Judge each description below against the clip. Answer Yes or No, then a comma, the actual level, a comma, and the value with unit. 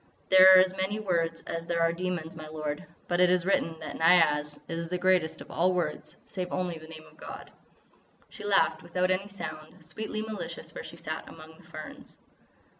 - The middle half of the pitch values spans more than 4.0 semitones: No, narrow, 2.6 semitones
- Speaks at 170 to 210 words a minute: Yes, average, 195 wpm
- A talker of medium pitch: Yes, medium, 170 Hz